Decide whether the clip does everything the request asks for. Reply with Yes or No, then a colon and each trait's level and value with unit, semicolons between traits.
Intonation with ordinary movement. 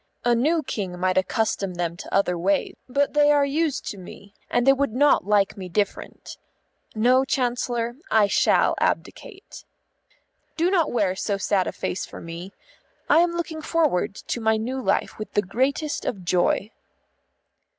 No: wide, 6.4 semitones